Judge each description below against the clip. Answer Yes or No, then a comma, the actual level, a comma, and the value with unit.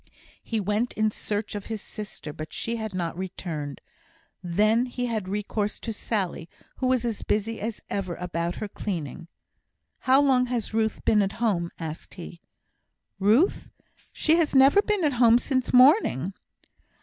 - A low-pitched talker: No, high, 215 Hz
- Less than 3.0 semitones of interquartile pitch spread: No, average, 4.8 semitones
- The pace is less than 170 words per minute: Yes, average, 160 wpm